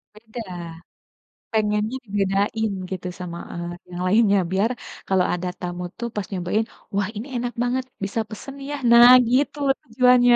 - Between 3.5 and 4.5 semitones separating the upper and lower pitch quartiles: Yes, average, 4.1 semitones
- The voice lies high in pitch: Yes, high, 215 Hz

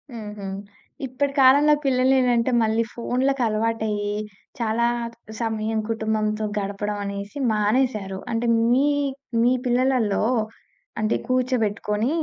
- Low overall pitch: No, high, 225 Hz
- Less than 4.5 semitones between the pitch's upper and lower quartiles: Yes, average, 3.2 semitones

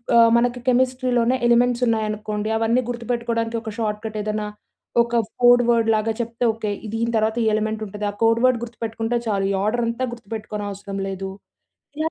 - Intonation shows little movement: Yes, narrow, 1.9 semitones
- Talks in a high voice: Yes, high, 230 Hz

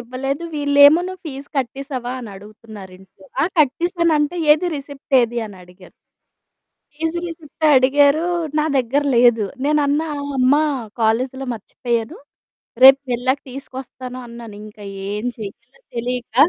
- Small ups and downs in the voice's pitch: No, average, 3.7 semitones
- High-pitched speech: Yes, very high, 260 Hz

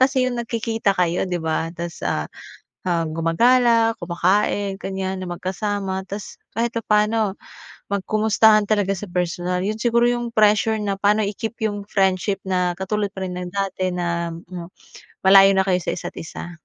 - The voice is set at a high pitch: Yes, high, 195 Hz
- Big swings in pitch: No, average, 3.1 semitones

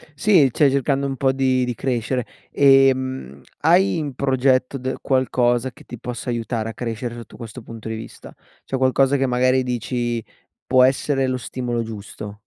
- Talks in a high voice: No, low, 130 Hz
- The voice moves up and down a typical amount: No, narrow, 2.2 semitones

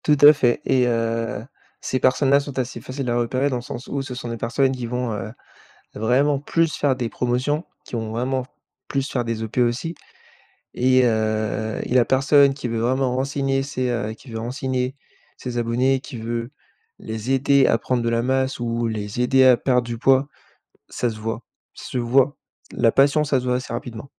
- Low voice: Yes, low, 125 Hz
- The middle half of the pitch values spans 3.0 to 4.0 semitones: No, narrow, 2.4 semitones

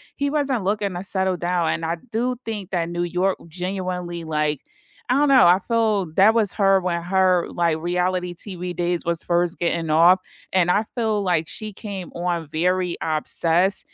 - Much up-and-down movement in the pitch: No, narrow, 2.5 semitones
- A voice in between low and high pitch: Yes, medium, 180 Hz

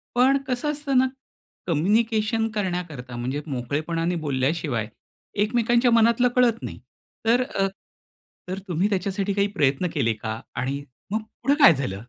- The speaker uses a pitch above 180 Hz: Yes, high, 190 Hz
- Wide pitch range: Yes, wide, 8.6 semitones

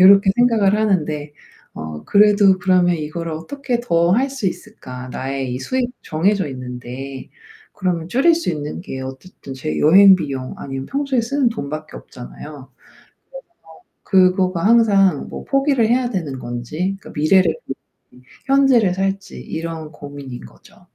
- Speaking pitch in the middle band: Yes, medium, 180 Hz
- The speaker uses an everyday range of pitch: No, wide, 7.2 semitones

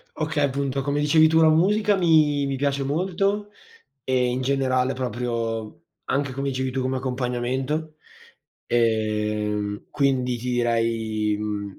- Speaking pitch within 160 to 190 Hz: No, low, 130 Hz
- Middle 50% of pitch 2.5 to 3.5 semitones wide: No, average, 3.9 semitones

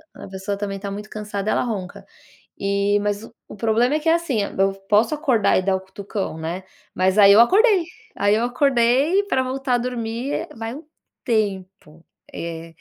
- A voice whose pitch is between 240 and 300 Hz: No, high, 215 Hz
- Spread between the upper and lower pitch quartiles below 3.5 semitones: No, average, 4.3 semitones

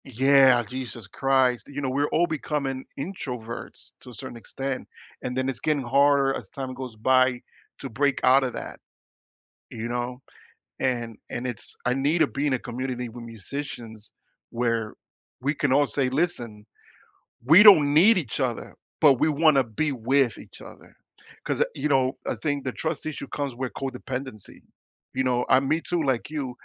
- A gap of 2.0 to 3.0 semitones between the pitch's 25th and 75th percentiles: Yes, average, 2.7 semitones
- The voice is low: Yes, low, 130 Hz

